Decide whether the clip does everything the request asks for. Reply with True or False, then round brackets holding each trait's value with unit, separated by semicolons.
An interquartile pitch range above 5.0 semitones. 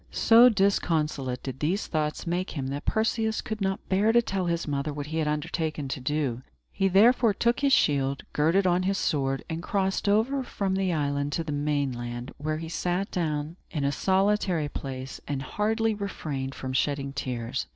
True (5.6 semitones)